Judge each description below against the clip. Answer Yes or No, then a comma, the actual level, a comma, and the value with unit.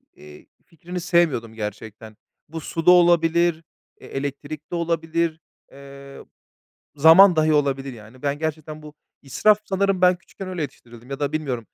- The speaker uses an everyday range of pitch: Yes, average, 3.8 semitones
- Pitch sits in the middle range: Yes, medium, 155 Hz